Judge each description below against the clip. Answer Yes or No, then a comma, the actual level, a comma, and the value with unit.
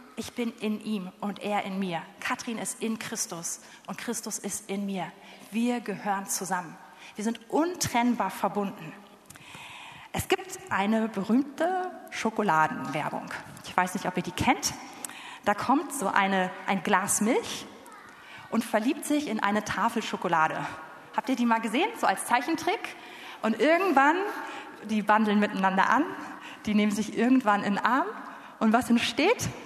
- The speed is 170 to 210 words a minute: No, average, 150 wpm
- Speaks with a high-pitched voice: Yes, high, 215 Hz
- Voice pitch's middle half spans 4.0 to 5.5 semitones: Yes, average, 4.3 semitones